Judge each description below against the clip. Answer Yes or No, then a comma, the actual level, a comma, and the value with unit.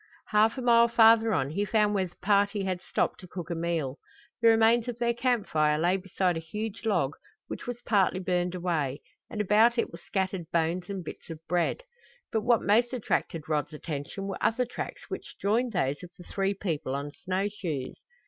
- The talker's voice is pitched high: Yes, high, 195 Hz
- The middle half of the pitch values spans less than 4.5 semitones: No, average, 4.8 semitones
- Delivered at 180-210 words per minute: Yes, average, 200 wpm